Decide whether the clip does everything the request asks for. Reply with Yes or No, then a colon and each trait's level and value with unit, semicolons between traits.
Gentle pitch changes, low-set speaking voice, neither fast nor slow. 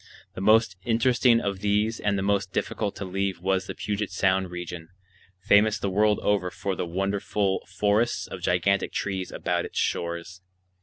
Yes: narrow, 1.8 semitones; low, 100 Hz; average, 165 wpm